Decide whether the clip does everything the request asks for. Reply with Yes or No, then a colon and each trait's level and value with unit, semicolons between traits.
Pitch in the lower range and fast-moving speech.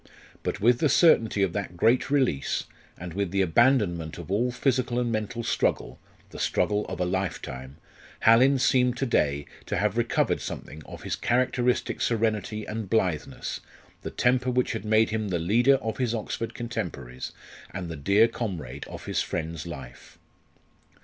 No: low, 110 Hz; average, 165 wpm